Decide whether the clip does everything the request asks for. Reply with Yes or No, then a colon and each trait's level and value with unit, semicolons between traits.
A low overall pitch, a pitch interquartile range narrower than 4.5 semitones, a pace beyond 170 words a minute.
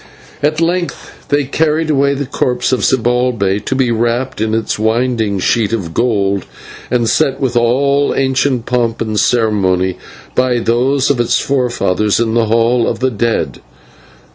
No: low, 120 Hz; average, 3.0 semitones; average, 155 wpm